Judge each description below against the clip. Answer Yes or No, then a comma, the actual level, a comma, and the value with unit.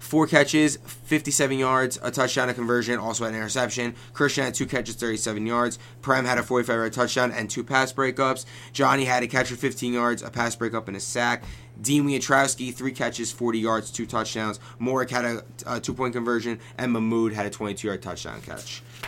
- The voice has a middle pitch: No, low, 120 Hz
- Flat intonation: Yes, narrow, 2.0 semitones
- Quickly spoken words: No, average, 190 wpm